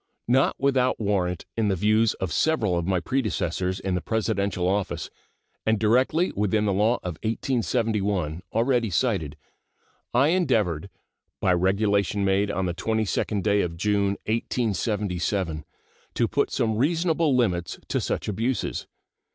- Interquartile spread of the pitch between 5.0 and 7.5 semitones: No, average, 3.8 semitones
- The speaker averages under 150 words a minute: Yes, slow, 135 wpm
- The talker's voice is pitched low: Yes, low, 105 Hz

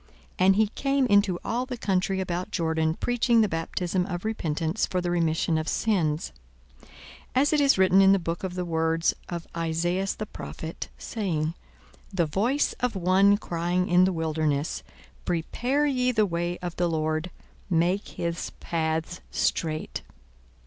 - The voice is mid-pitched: Yes, medium, 180 Hz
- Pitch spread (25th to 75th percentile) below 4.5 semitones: Yes, average, 3.6 semitones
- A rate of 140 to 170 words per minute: Yes, average, 160 wpm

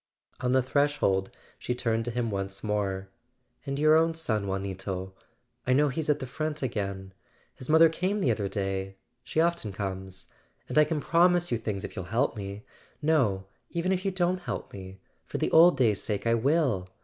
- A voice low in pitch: Yes, low, 120 Hz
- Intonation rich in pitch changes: Yes, wide, 7.9 semitones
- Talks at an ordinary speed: Yes, average, 180 wpm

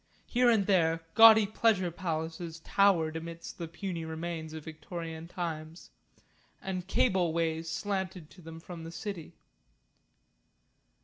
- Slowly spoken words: Yes, slow, 125 wpm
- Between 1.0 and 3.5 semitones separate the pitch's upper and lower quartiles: Yes, average, 2.8 semitones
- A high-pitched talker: No, medium, 170 Hz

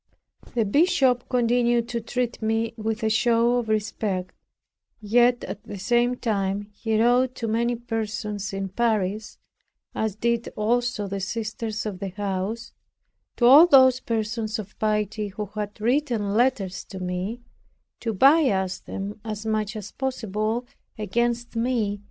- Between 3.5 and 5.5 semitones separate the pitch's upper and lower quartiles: No, narrow, 2.6 semitones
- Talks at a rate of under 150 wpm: Yes, average, 140 wpm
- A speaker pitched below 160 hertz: No, high, 220 Hz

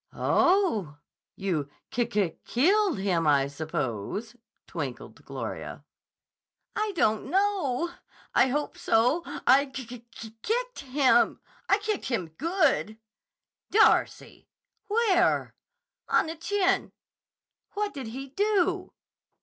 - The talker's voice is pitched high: Yes, very high, 275 Hz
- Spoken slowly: Yes, slow, 105 wpm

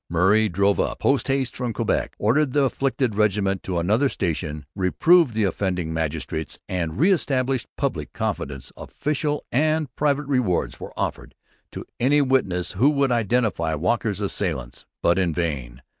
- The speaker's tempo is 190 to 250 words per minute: No, average, 150 wpm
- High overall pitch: No, low, 105 Hz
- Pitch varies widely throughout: Yes, wide, 7.7 semitones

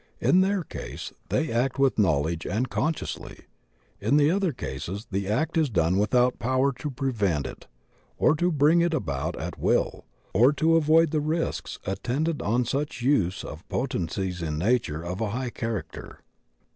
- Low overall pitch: Yes, low, 125 Hz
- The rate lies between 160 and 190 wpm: Yes, average, 165 wpm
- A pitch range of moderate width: No, wide, 8.1 semitones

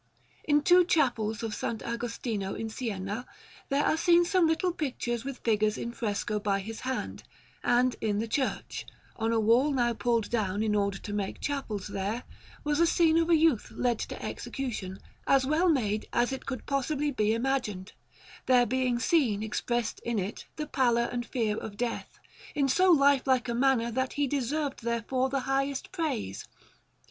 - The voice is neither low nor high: No, high, 245 Hz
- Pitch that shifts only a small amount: No, average, 4.1 semitones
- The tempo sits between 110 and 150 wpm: No, average, 175 wpm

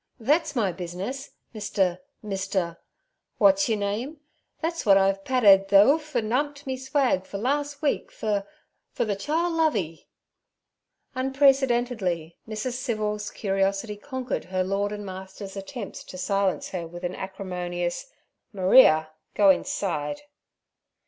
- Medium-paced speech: No, slow, 120 wpm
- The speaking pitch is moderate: No, high, 210 Hz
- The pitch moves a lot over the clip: Yes, wide, 5.8 semitones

